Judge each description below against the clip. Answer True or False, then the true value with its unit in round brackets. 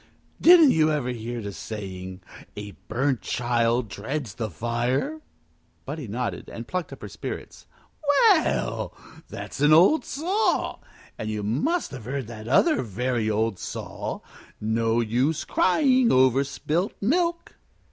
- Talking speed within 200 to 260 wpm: False (135 wpm)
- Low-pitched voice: True (125 Hz)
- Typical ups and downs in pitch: False (8.3 semitones)